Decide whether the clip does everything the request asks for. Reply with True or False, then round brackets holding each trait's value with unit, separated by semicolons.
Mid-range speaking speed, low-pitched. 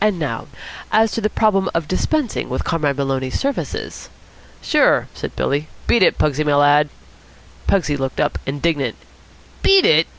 False (155 wpm; 155 Hz)